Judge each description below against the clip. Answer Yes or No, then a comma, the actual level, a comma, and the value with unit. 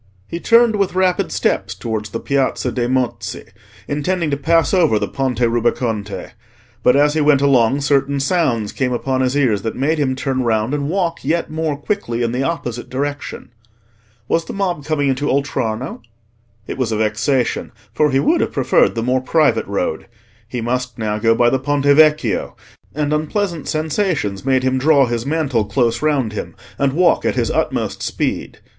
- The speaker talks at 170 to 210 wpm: Yes, average, 180 wpm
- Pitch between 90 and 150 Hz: Yes, low, 135 Hz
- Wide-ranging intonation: No, average, 4.3 semitones